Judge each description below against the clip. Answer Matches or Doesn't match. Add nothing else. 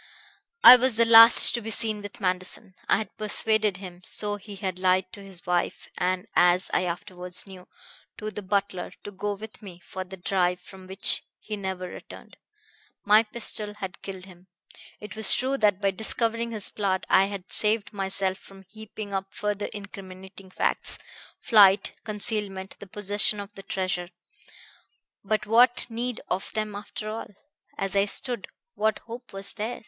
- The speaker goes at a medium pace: Matches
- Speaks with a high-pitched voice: Matches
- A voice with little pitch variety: Matches